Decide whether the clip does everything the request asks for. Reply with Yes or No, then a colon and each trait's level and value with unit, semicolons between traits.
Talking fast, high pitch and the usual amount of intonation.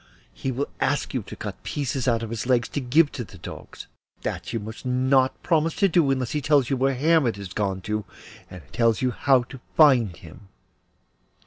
No: fast, 210 wpm; low, 125 Hz; average, 4.0 semitones